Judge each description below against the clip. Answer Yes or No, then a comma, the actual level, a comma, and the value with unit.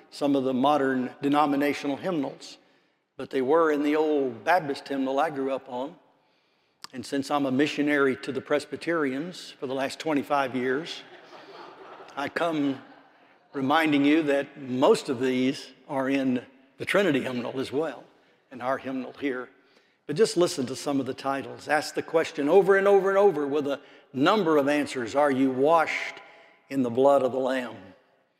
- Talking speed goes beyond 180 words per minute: No, average, 170 wpm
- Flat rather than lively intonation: Yes, narrow, 1.8 semitones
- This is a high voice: No, medium, 140 Hz